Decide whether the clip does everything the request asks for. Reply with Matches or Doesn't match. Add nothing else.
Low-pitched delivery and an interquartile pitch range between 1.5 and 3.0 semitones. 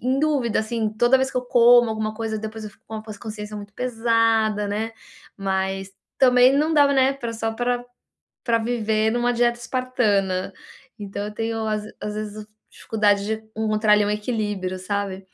Doesn't match